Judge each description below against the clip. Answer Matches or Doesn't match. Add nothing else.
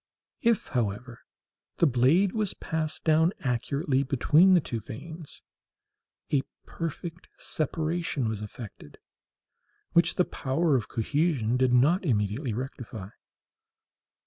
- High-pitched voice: Doesn't match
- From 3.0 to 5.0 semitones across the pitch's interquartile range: Doesn't match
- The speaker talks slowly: Matches